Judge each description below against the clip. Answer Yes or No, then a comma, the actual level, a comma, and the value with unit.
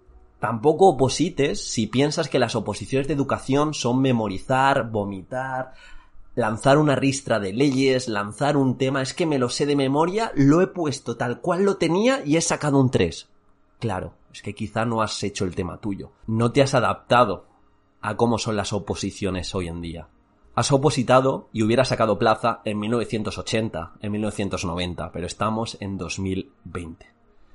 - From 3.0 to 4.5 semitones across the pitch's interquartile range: No, average, 5.0 semitones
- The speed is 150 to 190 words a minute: Yes, average, 165 wpm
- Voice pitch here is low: Yes, low, 120 Hz